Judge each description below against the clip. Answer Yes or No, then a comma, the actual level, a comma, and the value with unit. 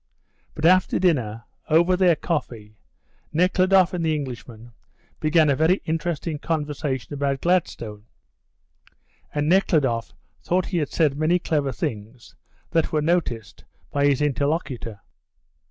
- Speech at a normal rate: No, slow, 120 wpm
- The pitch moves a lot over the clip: No, average, 4.4 semitones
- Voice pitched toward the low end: No, medium, 150 Hz